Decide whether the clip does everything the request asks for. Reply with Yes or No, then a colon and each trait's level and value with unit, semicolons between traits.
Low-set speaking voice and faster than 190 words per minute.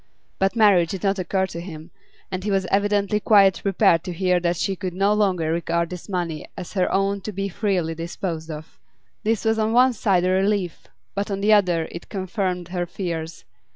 No: high, 190 Hz; average, 200 wpm